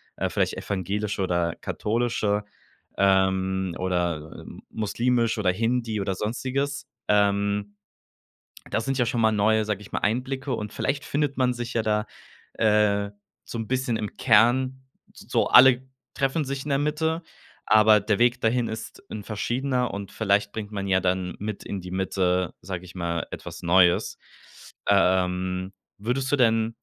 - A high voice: No, low, 105 Hz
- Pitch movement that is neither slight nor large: Yes, average, 4.3 semitones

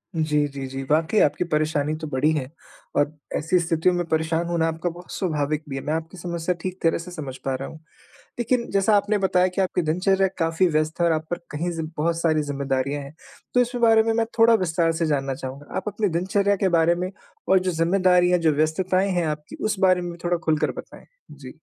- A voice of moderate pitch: Yes, medium, 165 Hz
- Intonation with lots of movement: No, average, 3.2 semitones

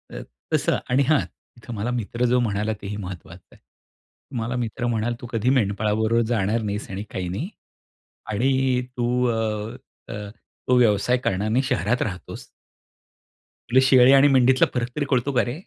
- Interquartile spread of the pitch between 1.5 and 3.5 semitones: Yes, average, 3.1 semitones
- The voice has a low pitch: Yes, low, 115 Hz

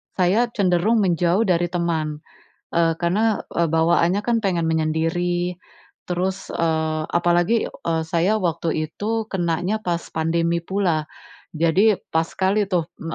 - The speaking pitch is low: No, medium, 175 Hz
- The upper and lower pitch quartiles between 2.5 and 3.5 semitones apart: Yes, average, 2.8 semitones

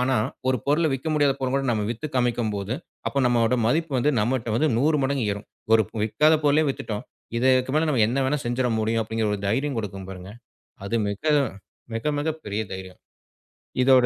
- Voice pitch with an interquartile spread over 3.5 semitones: Yes, average, 4.2 semitones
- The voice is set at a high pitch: No, low, 125 Hz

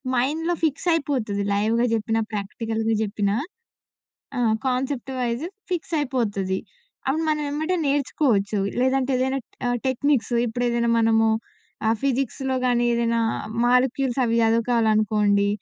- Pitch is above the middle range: Yes, high, 240 Hz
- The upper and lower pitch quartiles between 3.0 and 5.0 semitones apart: Yes, average, 3.3 semitones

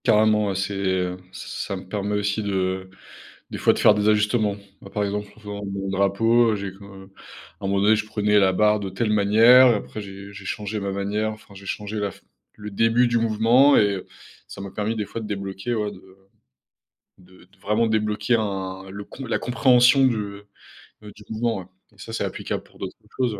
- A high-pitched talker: No, low, 105 Hz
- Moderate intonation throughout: No, narrow, 1.9 semitones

